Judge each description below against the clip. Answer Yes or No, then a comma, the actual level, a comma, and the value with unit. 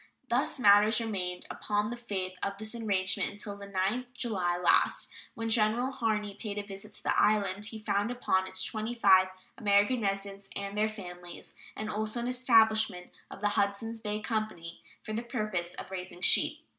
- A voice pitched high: Yes, high, 210 Hz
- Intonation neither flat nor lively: No, narrow, 2.3 semitones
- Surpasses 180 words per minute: No, average, 175 wpm